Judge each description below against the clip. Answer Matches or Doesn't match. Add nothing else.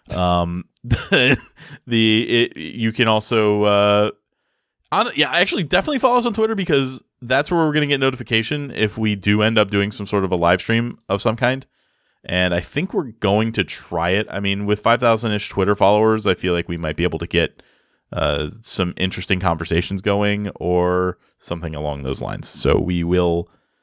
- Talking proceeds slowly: Doesn't match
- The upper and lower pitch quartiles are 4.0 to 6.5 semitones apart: Matches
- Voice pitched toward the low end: Matches